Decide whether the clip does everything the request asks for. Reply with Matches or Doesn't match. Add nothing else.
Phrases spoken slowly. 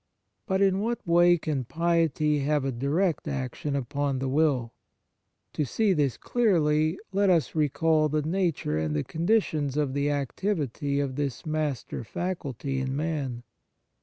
Doesn't match